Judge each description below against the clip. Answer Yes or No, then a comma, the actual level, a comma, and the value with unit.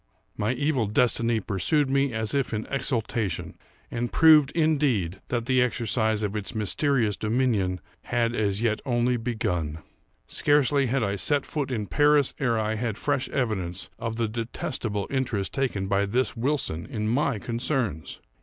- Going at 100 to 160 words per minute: Yes, average, 155 wpm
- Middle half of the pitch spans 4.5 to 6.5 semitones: No, average, 4.1 semitones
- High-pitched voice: No, low, 115 Hz